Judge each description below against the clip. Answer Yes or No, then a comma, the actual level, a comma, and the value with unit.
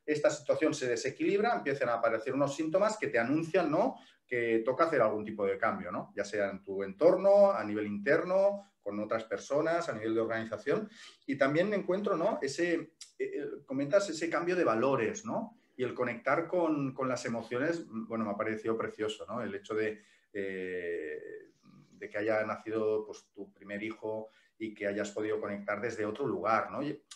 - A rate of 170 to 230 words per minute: Yes, average, 185 wpm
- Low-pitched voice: Yes, low, 115 Hz